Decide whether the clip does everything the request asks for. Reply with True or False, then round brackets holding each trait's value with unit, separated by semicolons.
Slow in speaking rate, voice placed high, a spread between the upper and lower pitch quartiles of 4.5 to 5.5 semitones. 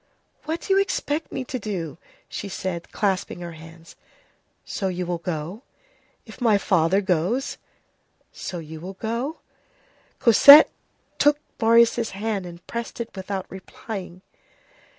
True (130 wpm; 195 Hz; 4.9 semitones)